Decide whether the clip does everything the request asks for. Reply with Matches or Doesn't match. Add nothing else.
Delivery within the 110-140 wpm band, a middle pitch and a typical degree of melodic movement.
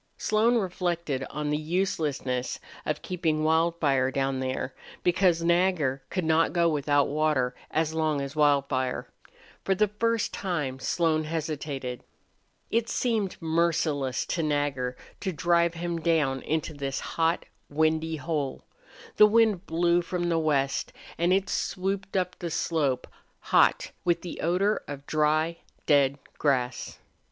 Matches